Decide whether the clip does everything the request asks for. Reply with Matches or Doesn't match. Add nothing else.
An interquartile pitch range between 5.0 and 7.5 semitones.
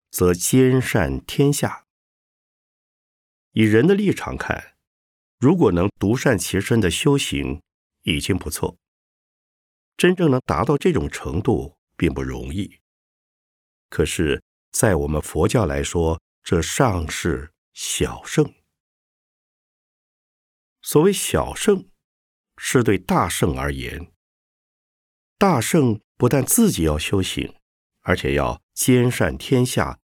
Doesn't match